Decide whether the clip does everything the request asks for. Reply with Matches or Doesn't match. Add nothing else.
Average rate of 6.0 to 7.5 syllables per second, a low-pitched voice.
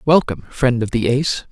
Matches